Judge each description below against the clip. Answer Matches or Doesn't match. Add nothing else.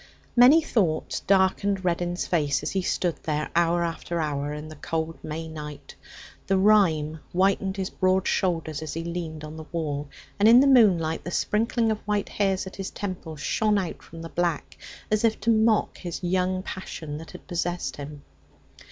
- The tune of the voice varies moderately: Matches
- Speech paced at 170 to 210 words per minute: Matches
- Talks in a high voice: Doesn't match